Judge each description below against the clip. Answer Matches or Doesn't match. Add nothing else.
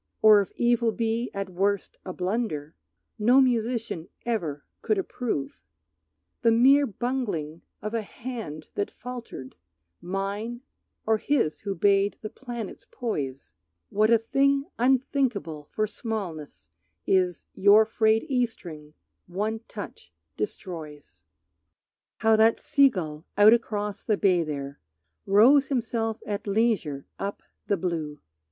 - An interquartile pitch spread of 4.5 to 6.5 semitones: Matches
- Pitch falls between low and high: Doesn't match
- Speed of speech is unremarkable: Doesn't match